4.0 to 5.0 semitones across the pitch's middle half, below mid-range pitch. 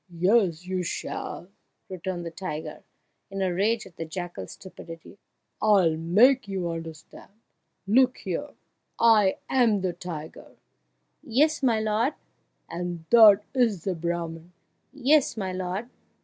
No: average, 4.4 semitones; high, 190 Hz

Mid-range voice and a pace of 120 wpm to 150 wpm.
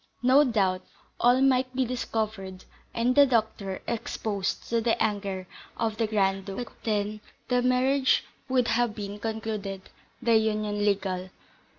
No: high, 220 Hz; average, 145 wpm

